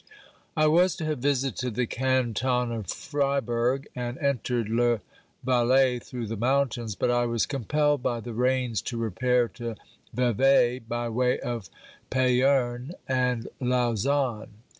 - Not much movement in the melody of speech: Yes, narrow, 2.0 semitones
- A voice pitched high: No, low, 125 Hz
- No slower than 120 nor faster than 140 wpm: Yes, slow, 135 wpm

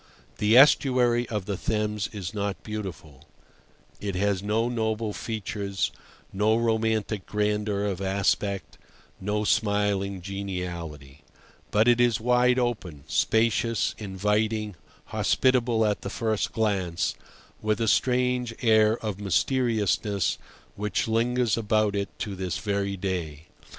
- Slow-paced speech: Yes, slow, 120 wpm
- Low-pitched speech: Yes, low, 105 Hz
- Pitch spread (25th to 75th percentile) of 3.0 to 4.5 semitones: No, narrow, 2.4 semitones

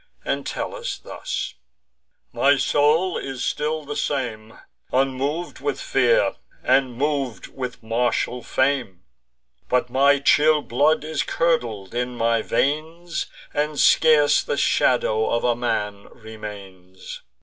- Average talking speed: No, slow, 115 wpm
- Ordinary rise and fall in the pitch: Yes, average, 4.4 semitones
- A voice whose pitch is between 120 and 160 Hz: Yes, low, 135 Hz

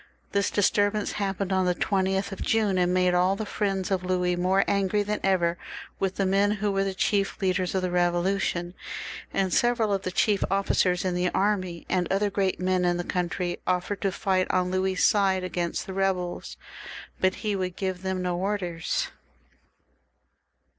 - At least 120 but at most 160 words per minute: No, average, 180 wpm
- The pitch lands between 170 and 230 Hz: Yes, high, 190 Hz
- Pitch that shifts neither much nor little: No, narrow, 1.6 semitones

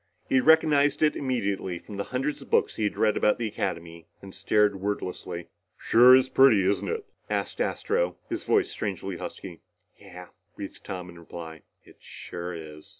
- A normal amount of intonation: No, wide, 6.9 semitones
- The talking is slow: No, average, 170 wpm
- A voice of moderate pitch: No, low, 105 Hz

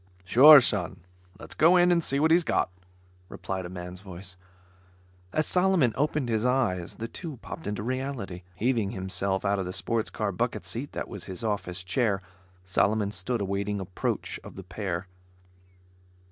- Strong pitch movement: Yes, wide, 5.8 semitones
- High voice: No, low, 105 Hz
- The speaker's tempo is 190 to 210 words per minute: No, average, 165 wpm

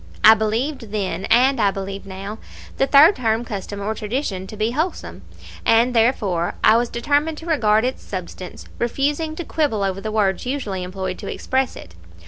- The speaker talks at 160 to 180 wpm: Yes, average, 175 wpm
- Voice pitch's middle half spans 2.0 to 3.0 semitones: No, average, 5.2 semitones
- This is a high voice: Yes, high, 220 Hz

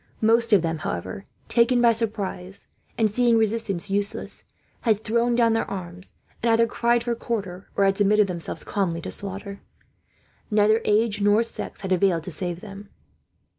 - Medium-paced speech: Yes, average, 165 wpm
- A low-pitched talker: No, high, 205 Hz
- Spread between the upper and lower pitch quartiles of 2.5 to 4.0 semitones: Yes, average, 3.2 semitones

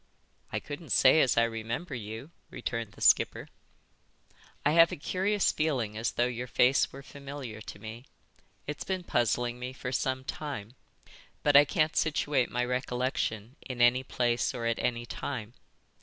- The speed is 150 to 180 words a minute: Yes, average, 160 wpm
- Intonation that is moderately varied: Yes, average, 3.5 semitones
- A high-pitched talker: No, low, 125 Hz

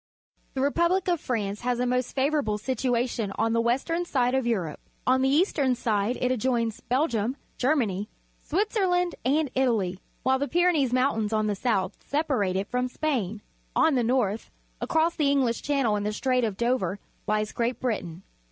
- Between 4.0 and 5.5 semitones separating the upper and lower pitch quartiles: Yes, average, 4.5 semitones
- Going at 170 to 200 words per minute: Yes, average, 180 wpm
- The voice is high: Yes, very high, 250 Hz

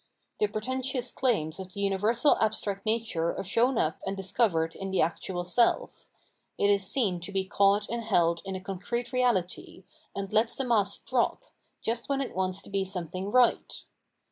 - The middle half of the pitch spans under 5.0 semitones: Yes, average, 4.0 semitones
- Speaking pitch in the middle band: No, high, 200 Hz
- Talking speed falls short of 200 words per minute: Yes, average, 180 wpm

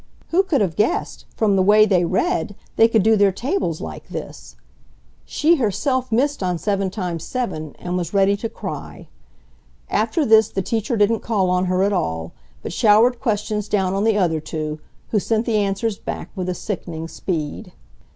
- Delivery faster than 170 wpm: Yes, average, 180 wpm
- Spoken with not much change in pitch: No, average, 3.6 semitones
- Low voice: No, high, 200 Hz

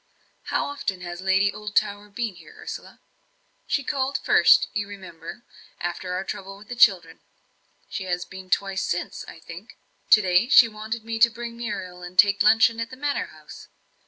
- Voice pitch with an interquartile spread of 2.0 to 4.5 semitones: Yes, average, 3.7 semitones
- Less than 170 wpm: No, average, 175 wpm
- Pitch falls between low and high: No, high, 205 Hz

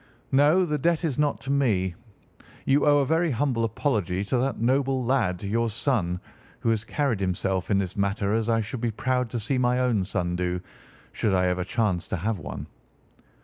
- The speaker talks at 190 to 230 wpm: Yes, average, 195 wpm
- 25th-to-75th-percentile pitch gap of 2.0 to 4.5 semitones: No, wide, 5.6 semitones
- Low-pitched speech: Yes, low, 115 Hz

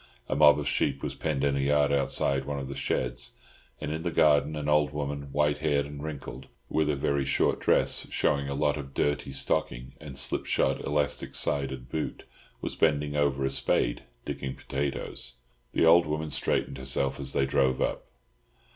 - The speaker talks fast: No, average, 180 wpm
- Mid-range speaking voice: No, very low, 70 Hz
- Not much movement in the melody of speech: Yes, narrow, 1.6 semitones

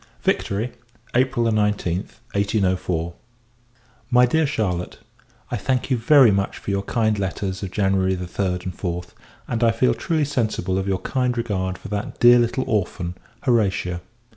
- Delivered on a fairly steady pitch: No, average, 4.4 semitones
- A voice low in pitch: Yes, low, 105 Hz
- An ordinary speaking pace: Yes, average, 150 wpm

